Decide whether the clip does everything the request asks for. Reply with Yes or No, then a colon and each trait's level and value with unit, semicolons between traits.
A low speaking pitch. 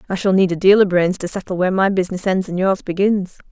No: high, 190 Hz